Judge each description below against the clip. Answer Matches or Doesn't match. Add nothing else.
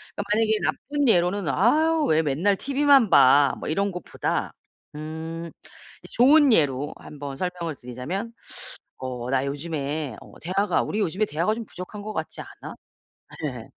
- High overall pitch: Doesn't match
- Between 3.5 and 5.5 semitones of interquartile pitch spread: Doesn't match